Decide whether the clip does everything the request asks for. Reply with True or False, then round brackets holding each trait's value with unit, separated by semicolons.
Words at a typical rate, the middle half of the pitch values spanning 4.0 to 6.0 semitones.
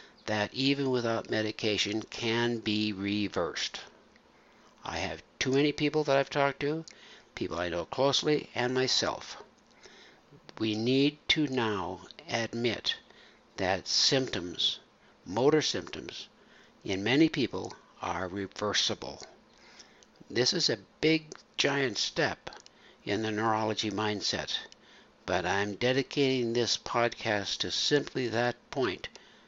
False (110 wpm; 4.3 semitones)